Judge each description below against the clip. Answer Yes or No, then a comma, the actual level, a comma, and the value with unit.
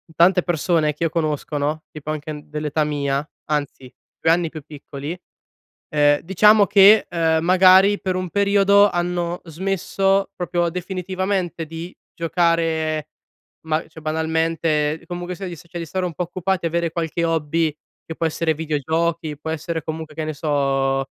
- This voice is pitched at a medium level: Yes, medium, 165 Hz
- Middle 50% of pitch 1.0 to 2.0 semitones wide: No, narrow, 2.5 semitones